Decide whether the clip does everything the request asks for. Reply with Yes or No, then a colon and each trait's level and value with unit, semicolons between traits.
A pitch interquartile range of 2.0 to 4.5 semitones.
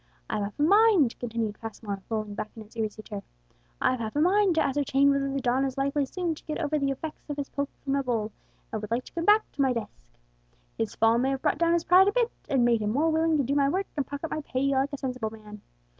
No: average, 5.1 semitones